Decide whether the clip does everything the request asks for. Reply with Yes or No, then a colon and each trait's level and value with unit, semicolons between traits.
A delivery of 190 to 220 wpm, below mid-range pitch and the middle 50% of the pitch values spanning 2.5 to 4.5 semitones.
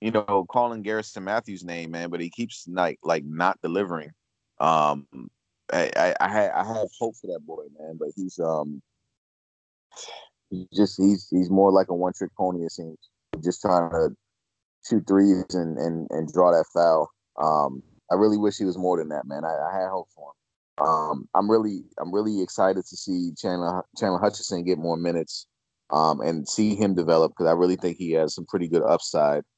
Yes: average, 195 wpm; very low, 90 Hz; average, 2.9 semitones